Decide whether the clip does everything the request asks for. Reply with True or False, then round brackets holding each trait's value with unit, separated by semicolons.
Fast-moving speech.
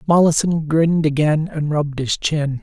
False (160 wpm)